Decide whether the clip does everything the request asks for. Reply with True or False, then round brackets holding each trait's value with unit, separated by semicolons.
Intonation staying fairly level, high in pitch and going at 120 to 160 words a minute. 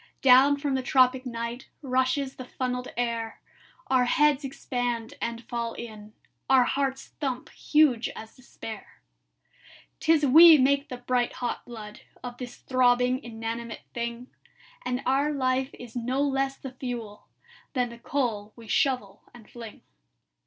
True (2.2 semitones; 250 Hz; 140 wpm)